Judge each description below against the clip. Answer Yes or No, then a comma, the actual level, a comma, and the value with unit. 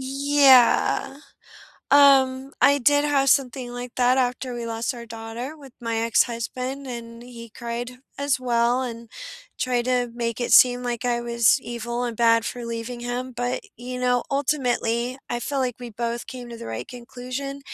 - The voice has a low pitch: No, high, 245 Hz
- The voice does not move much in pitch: Yes, narrow, 1.8 semitones